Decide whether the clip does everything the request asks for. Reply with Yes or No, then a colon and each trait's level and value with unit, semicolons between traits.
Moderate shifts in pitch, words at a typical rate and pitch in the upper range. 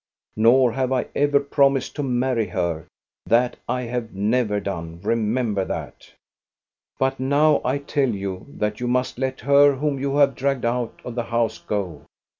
No: average, 3.9 semitones; average, 170 wpm; low, 125 Hz